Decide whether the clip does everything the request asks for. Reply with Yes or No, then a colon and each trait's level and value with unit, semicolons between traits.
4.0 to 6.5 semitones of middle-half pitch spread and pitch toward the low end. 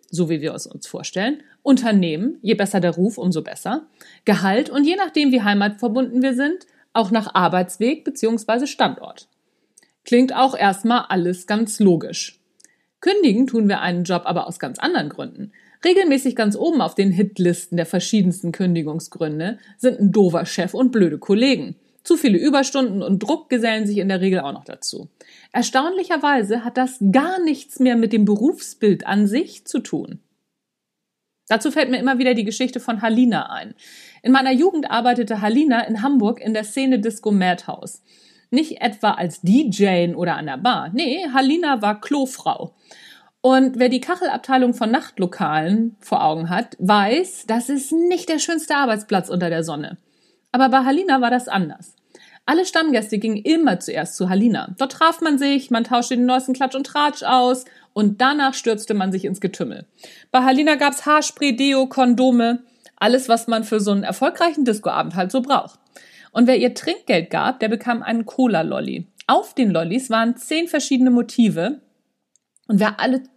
No: average, 4.9 semitones; high, 240 Hz